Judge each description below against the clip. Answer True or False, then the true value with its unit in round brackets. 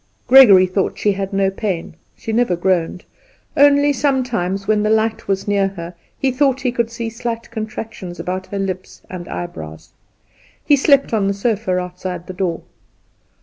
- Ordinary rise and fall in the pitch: True (4.2 semitones)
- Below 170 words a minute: True (160 wpm)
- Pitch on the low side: False (200 Hz)